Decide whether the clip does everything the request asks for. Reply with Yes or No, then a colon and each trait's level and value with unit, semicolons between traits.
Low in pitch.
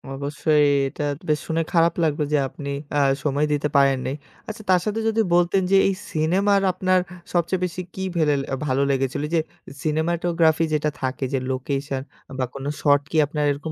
No: medium, 155 Hz